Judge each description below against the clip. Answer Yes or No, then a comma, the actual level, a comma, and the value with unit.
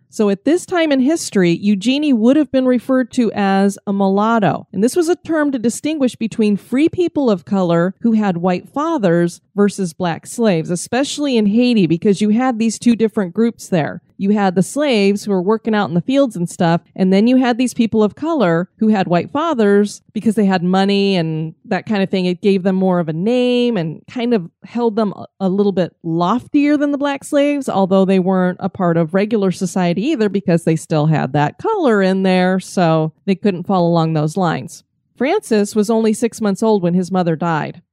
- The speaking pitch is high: Yes, high, 200 Hz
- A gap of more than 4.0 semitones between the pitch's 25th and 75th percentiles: Yes, average, 4.5 semitones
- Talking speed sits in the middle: No, fast, 210 wpm